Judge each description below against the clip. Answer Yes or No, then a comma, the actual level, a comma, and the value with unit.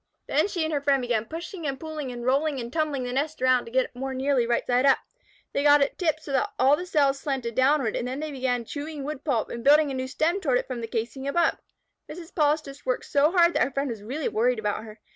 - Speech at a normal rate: No, fast, 260 wpm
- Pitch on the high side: Yes, very high, 275 Hz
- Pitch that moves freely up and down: No, average, 3.5 semitones